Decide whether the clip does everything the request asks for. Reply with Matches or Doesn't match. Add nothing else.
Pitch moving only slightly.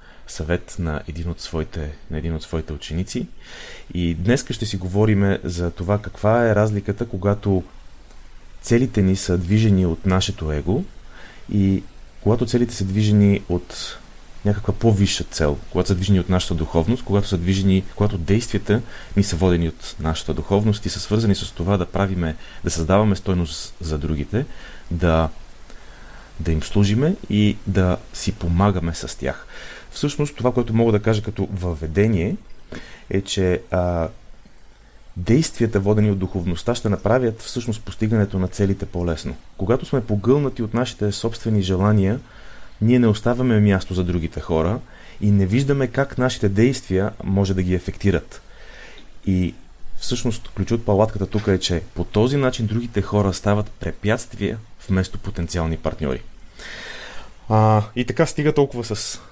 Doesn't match